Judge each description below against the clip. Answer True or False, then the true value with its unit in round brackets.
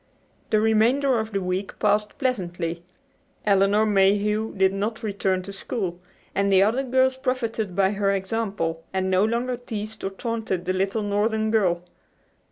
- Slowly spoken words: False (155 wpm)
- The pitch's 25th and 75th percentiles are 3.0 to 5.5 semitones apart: False (2.6 semitones)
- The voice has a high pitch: True (205 Hz)